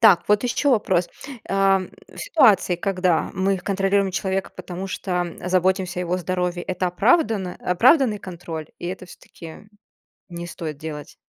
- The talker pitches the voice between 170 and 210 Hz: Yes, medium, 185 Hz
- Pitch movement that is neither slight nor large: No, narrow, 2.0 semitones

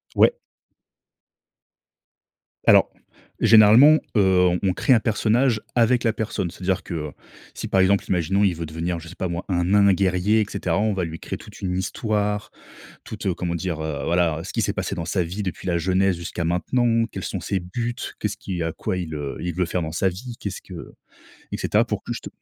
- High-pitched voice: No, very low, 95 Hz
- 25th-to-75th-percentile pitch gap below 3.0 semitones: No, average, 3.3 semitones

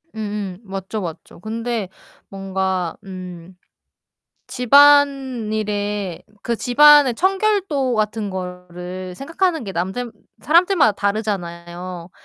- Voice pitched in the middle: No, high, 210 Hz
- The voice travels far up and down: Yes, wide, 5.7 semitones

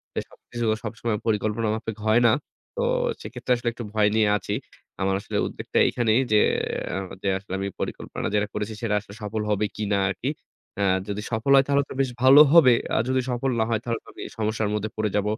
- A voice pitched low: Yes, low, 110 Hz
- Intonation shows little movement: Yes, narrow, 2.3 semitones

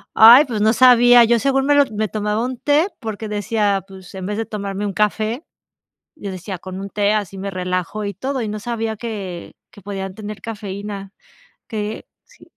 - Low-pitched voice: No, high, 210 Hz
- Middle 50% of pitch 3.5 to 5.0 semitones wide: No, narrow, 2.6 semitones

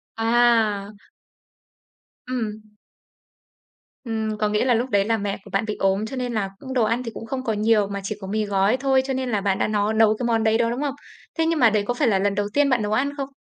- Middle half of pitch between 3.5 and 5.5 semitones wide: No, average, 3.1 semitones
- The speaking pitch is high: Yes, high, 225 Hz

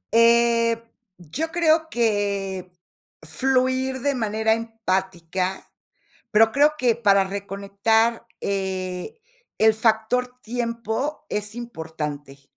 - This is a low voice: No, high, 220 Hz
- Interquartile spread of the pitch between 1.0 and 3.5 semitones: No, average, 3.9 semitones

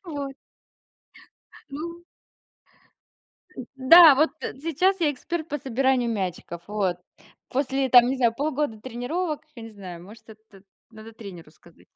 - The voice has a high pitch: Yes, very high, 255 Hz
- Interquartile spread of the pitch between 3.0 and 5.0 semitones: No, wide, 5.4 semitones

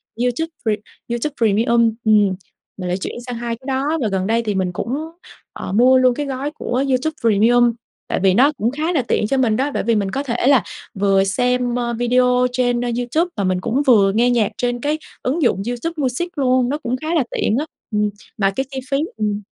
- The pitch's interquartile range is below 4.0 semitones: Yes, average, 3.5 semitones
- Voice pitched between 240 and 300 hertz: Yes, high, 245 Hz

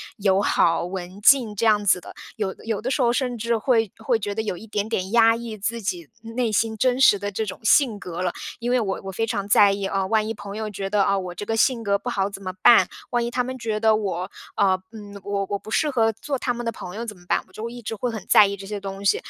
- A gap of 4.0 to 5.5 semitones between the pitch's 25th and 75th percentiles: No, average, 2.8 semitones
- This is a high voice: Yes, high, 215 Hz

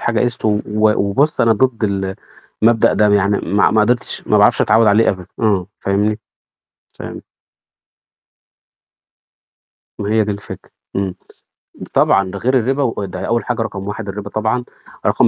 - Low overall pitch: Yes, low, 105 Hz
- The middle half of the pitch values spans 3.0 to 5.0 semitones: No, narrow, 2.4 semitones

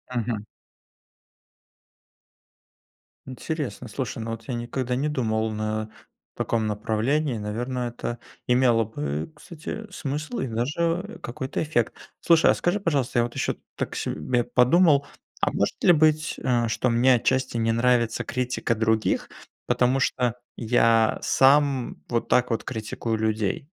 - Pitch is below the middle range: Yes, low, 120 Hz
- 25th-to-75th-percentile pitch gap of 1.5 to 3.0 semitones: No, average, 3.5 semitones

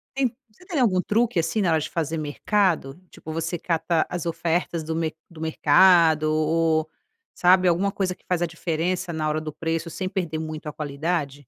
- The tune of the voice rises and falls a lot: No, narrow, 2.5 semitones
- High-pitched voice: No, medium, 165 Hz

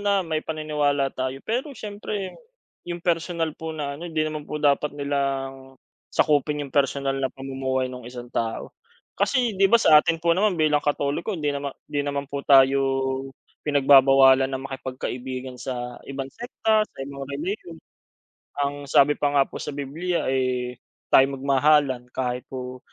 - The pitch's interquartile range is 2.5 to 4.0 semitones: Yes, average, 2.9 semitones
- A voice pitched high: No, medium, 140 Hz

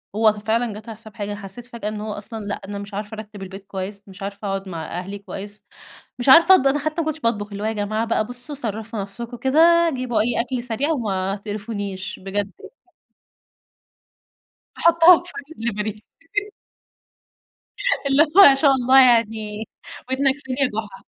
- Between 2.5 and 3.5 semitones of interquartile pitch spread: No, average, 4.0 semitones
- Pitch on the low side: No, high, 220 Hz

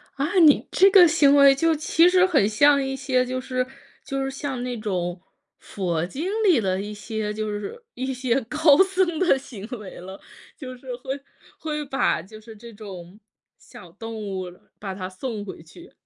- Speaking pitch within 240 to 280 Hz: Yes, very high, 255 Hz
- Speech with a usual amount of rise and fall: No, wide, 5.8 semitones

